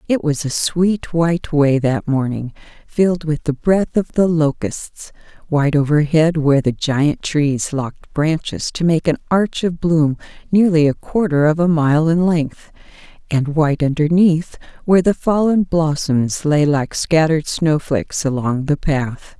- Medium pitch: Yes, medium, 155 Hz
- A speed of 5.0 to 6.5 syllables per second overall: No, 4.3 syllables/s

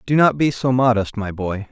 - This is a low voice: Yes, low, 120 Hz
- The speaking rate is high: Yes, fast, 245 wpm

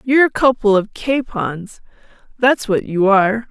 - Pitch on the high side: Yes, high, 220 Hz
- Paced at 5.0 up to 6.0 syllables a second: No, 4.6 syllables/s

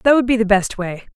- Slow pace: No, fast, 315 wpm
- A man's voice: No, female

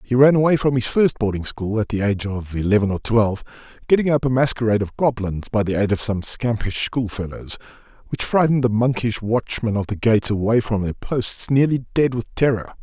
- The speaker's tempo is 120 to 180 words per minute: No, fast, 205 wpm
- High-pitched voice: No, low, 115 Hz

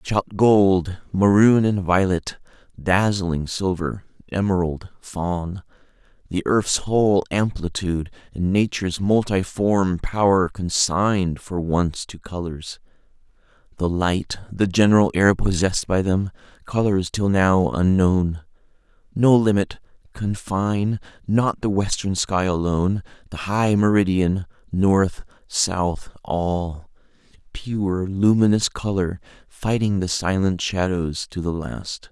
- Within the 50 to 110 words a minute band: Yes, slow, 105 wpm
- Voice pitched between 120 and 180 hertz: No, very low, 95 Hz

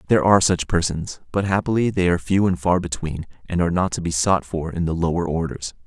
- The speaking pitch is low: Yes, very low, 90 Hz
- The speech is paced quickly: Yes, fast, 235 wpm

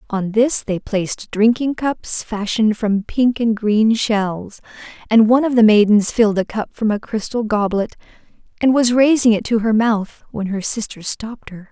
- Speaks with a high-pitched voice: Yes, high, 220 Hz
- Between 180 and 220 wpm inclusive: Yes, average, 185 wpm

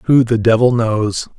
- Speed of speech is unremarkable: Yes, average, 175 wpm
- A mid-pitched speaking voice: No, low, 115 Hz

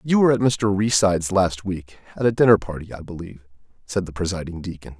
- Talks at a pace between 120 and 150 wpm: No, fast, 205 wpm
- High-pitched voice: No, very low, 95 Hz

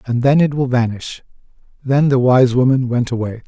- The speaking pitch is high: No, low, 125 Hz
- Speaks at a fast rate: No, average, 190 wpm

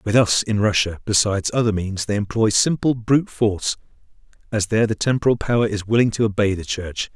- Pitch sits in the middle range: No, low, 110 Hz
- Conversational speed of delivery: Yes, average, 195 wpm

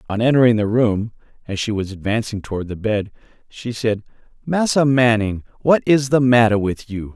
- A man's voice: Yes, male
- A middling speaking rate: Yes, average, 175 wpm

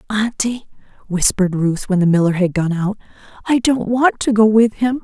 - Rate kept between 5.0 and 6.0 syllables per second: Yes, 5.3 syllables/s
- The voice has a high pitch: Yes, high, 210 Hz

